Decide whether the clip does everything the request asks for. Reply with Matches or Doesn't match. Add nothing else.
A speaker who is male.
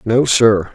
Matches